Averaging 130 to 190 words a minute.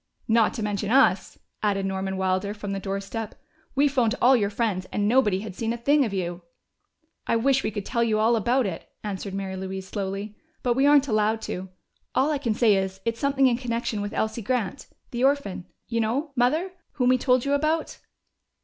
No: fast, 205 wpm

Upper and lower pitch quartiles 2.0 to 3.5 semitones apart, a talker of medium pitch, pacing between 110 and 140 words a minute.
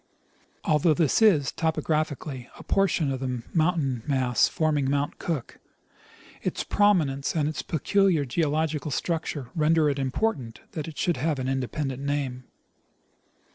Yes: average, 3.2 semitones; medium, 150 Hz; slow, 135 wpm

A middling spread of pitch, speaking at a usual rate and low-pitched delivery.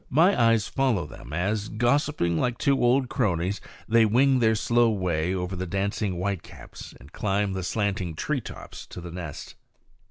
Yes: average, 4.9 semitones; average, 165 wpm; low, 105 Hz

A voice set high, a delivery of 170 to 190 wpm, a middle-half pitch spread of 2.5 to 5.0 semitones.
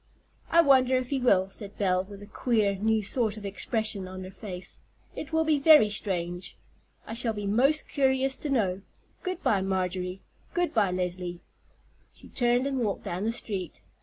No: high, 210 Hz; average, 175 wpm; wide, 5.5 semitones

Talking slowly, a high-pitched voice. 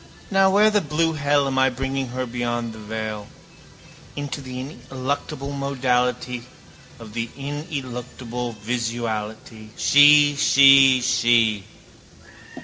No: slow, 110 wpm; low, 130 Hz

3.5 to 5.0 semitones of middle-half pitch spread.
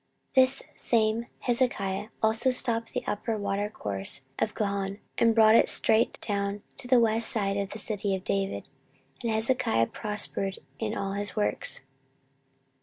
No: narrow, 2.5 semitones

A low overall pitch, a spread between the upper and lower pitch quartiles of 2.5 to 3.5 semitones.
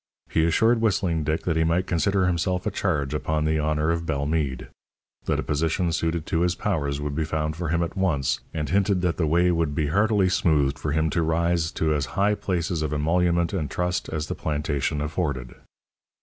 Yes: very low, 80 Hz; average, 2.8 semitones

